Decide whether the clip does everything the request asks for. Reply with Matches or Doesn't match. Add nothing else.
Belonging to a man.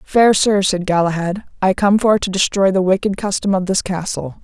Doesn't match